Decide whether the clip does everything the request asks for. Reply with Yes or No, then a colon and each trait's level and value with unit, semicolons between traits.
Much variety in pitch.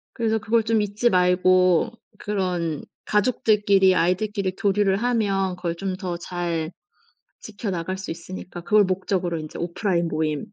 No: average, 3.0 semitones